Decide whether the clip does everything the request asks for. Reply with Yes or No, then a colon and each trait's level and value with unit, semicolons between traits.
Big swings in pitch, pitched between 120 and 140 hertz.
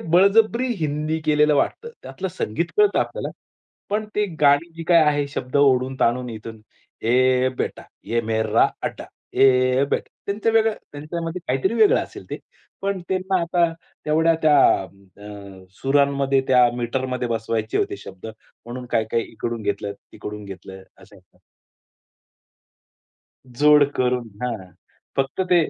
Yes: wide, 6.1 semitones; low, 135 Hz